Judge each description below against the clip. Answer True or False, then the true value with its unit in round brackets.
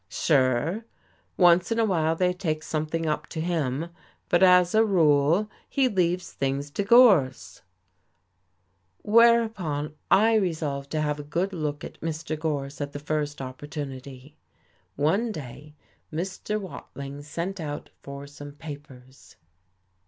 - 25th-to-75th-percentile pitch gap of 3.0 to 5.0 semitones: True (4.1 semitones)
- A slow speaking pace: True (130 wpm)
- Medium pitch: True (155 Hz)